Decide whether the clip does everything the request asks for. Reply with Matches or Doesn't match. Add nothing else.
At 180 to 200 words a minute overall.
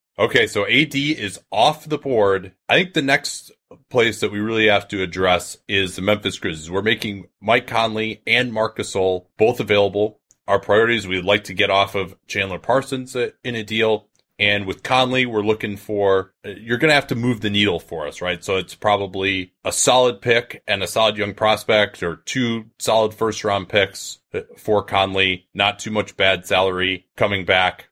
Matches